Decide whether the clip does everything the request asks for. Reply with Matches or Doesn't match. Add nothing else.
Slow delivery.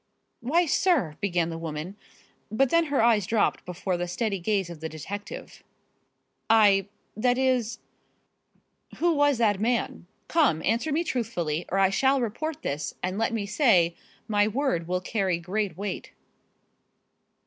Doesn't match